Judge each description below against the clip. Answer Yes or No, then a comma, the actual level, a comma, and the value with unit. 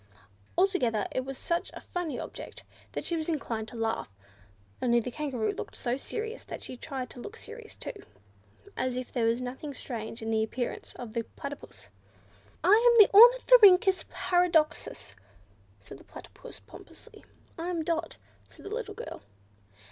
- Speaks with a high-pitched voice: Yes, very high, 290 Hz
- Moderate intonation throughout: No, wide, 7.9 semitones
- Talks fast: No, average, 165 wpm